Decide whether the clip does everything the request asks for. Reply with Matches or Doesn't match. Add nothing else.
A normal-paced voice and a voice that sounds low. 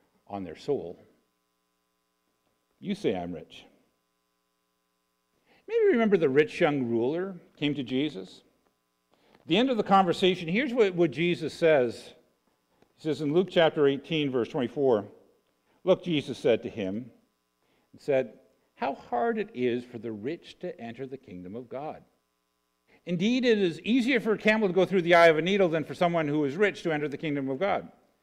Doesn't match